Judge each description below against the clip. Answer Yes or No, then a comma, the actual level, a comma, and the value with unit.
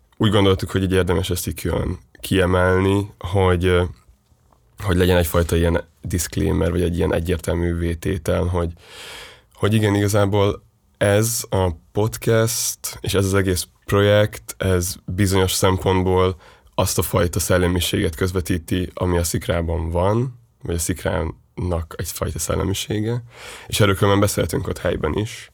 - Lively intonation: No, narrow, 2.6 semitones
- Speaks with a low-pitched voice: Yes, very low, 95 Hz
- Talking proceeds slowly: No, average, 130 wpm